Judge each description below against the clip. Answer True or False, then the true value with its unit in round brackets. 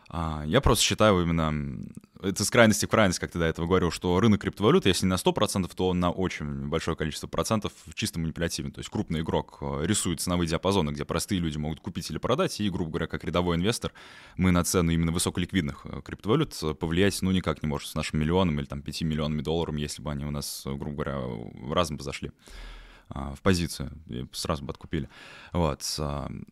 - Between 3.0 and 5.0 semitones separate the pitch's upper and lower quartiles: True (3.6 semitones)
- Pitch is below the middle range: True (85 Hz)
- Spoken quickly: True (195 wpm)